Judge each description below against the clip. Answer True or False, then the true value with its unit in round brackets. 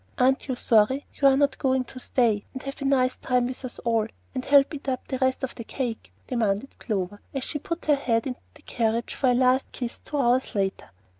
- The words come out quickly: True (230 wpm)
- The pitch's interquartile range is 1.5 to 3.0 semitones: True (2.6 semitones)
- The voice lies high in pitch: True (255 Hz)